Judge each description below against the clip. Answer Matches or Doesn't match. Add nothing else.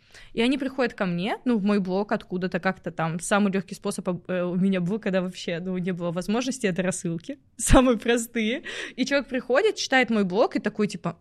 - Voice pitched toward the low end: Doesn't match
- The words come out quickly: Matches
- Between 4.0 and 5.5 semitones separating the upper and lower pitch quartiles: Matches